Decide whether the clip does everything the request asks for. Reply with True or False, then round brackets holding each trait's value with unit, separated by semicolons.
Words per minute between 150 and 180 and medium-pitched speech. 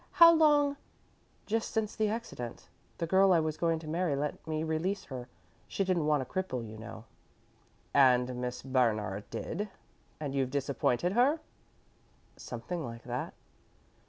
True (155 wpm; 155 Hz)